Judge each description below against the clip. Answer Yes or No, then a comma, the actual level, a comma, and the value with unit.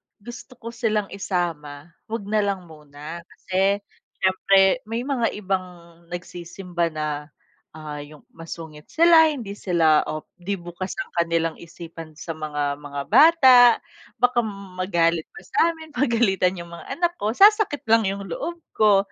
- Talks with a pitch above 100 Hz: Yes, high, 190 Hz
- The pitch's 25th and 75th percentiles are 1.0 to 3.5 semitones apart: No, wide, 5.5 semitones